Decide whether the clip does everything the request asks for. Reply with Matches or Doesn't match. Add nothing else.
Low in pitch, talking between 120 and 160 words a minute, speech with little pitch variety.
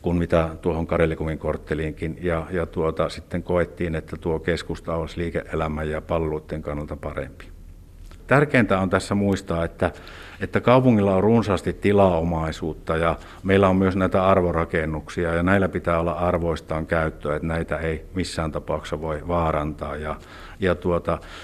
Matches